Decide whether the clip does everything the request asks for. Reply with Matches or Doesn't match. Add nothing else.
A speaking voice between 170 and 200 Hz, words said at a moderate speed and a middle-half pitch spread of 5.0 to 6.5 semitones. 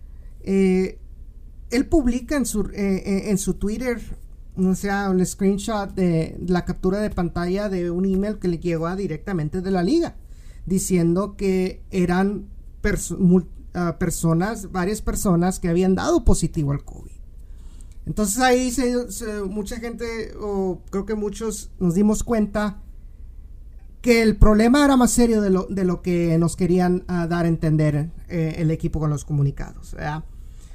Doesn't match